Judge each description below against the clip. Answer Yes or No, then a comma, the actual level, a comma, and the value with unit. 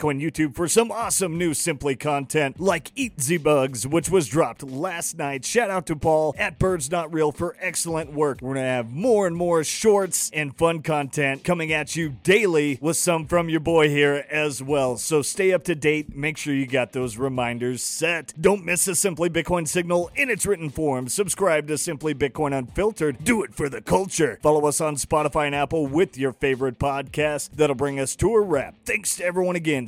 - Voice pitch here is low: No, medium, 155 Hz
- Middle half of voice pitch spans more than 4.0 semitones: No, average, 3.5 semitones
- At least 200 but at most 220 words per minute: Yes, fast, 205 wpm